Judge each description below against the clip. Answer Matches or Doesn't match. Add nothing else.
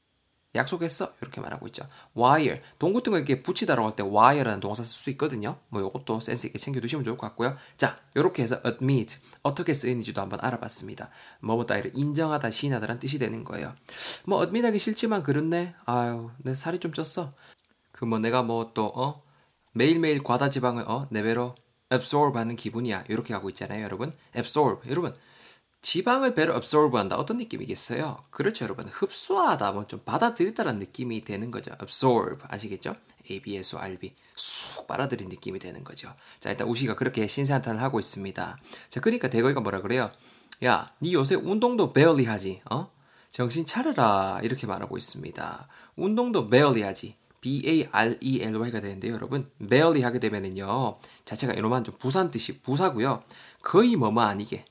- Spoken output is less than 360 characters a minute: Doesn't match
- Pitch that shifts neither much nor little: Matches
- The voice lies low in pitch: Matches